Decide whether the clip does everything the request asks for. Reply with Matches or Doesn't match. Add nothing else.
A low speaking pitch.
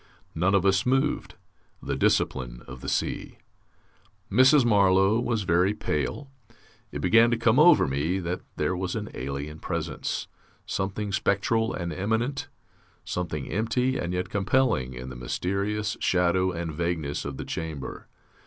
Matches